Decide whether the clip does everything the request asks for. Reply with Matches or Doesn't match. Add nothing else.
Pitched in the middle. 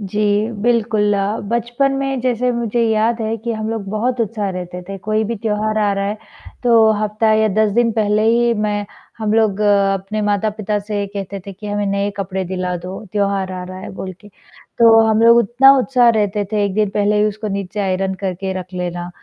Doesn't match